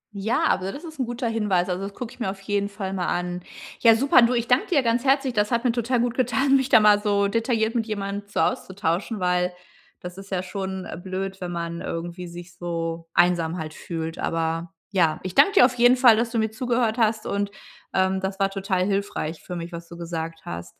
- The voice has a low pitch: No, high, 195 Hz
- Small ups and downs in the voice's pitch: No, average, 4.7 semitones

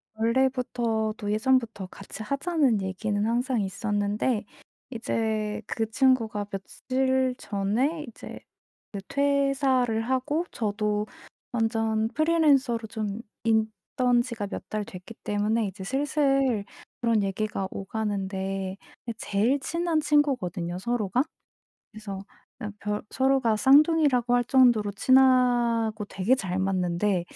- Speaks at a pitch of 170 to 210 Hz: No, high, 225 Hz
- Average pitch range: Yes, average, 4.0 semitones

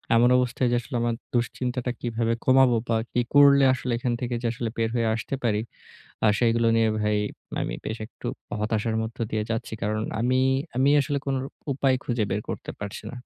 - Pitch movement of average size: No, narrow, 2.2 semitones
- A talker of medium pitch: No, low, 120 Hz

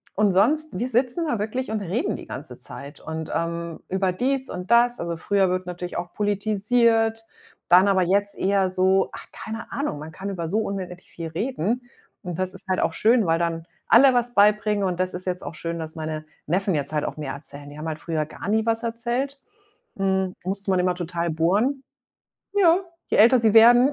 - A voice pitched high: Yes, high, 195 Hz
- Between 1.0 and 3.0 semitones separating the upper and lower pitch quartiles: No, average, 4.9 semitones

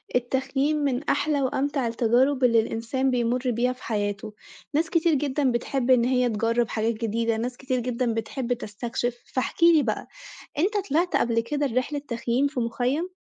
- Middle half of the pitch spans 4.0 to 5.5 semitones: No, average, 3.3 semitones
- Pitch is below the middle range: No, very high, 250 Hz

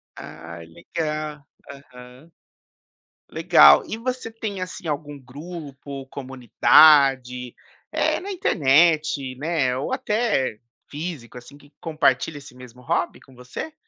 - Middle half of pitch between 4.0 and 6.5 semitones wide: Yes, average, 4.7 semitones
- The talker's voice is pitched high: No, medium, 145 Hz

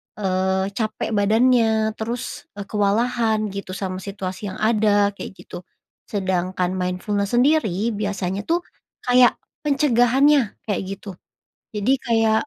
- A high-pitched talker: Yes, high, 210 Hz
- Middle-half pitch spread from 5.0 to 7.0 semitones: No, average, 3.3 semitones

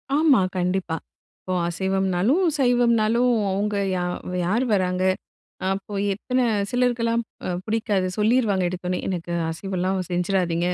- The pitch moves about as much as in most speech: Yes, average, 4.4 semitones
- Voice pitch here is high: Yes, high, 195 Hz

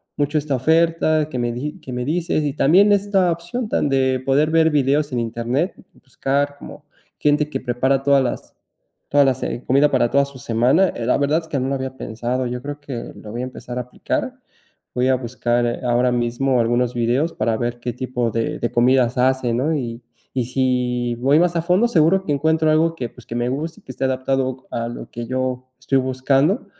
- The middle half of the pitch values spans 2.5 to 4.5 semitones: Yes, average, 3.4 semitones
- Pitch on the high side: No, low, 130 Hz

